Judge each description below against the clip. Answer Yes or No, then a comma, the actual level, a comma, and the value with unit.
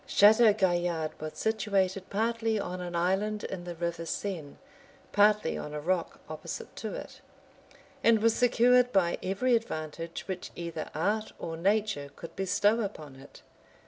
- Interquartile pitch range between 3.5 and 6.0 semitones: Yes, average, 4.2 semitones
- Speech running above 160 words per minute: No, average, 150 wpm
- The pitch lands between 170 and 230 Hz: Yes, high, 190 Hz